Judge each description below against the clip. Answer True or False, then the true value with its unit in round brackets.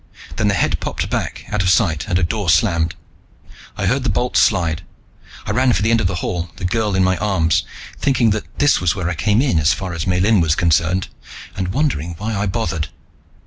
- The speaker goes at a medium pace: False (220 wpm)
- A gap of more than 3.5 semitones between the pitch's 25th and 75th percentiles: True (4.2 semitones)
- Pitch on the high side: False (95 Hz)